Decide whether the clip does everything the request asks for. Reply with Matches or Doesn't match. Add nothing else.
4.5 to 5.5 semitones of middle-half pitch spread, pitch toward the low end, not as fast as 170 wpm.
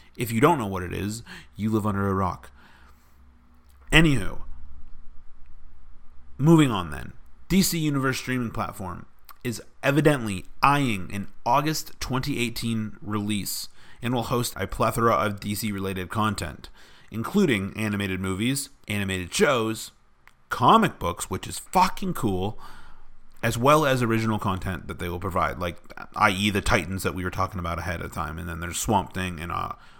Matches